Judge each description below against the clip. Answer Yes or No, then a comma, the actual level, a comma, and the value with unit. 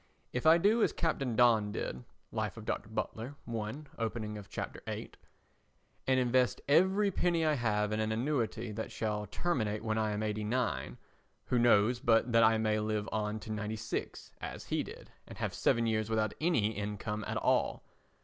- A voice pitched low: Yes, low, 110 Hz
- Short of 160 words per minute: No, average, 180 wpm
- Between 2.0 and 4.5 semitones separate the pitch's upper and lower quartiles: Yes, average, 2.8 semitones